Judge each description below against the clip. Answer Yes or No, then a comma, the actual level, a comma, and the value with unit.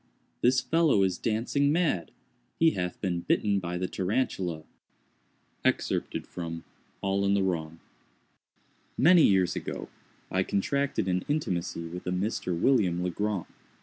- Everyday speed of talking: No, slow, 120 wpm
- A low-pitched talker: Yes, very low, 95 Hz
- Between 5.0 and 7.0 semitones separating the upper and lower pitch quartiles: Yes, wide, 5.4 semitones